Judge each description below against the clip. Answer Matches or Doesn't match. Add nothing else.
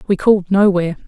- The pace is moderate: Matches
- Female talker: Matches